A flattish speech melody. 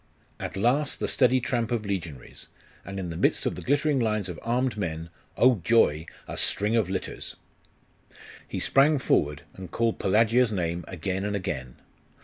No: wide, 5.5 semitones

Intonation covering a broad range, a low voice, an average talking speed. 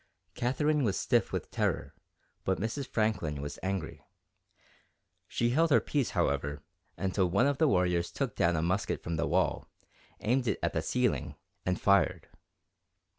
Yes: wide, 6.4 semitones; low, 100 Hz; average, 155 wpm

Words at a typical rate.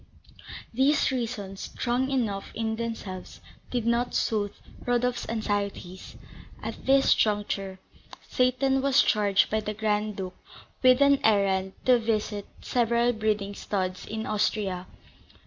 No: slow, 120 wpm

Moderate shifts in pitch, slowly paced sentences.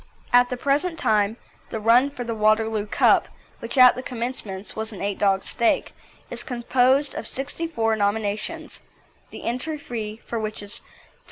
No: average, 3.2 semitones; average, 170 wpm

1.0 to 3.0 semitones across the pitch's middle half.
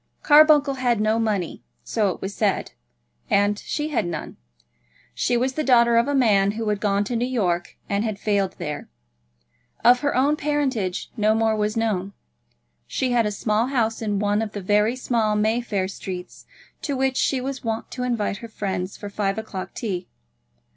No: average, 3.6 semitones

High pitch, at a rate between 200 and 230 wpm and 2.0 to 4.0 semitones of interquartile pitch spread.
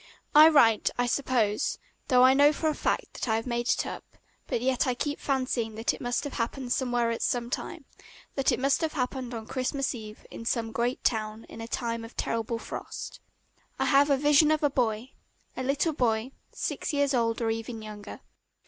Yes: high, 245 Hz; fast, 205 wpm; average, 3.3 semitones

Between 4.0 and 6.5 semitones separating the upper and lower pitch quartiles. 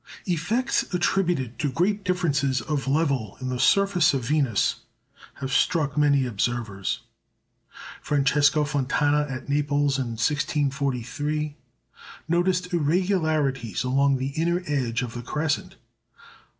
No: average, 3.5 semitones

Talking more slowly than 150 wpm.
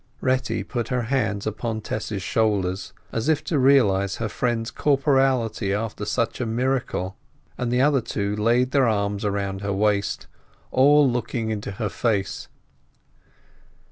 Yes: average, 140 wpm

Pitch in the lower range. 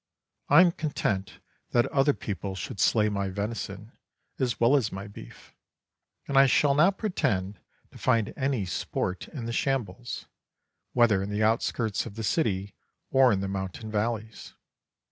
Yes: low, 110 Hz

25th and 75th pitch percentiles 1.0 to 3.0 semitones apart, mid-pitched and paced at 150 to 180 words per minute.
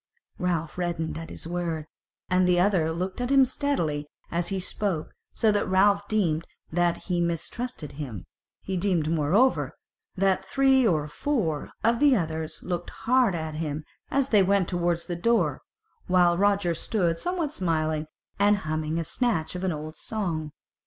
No: average, 4.2 semitones; medium, 175 Hz; average, 160 wpm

